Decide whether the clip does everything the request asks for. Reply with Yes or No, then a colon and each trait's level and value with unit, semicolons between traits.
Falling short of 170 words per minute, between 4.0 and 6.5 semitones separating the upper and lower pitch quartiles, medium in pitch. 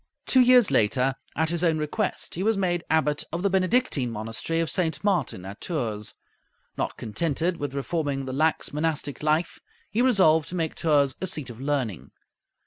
No: average, 175 wpm; average, 4.5 semitones; medium, 155 Hz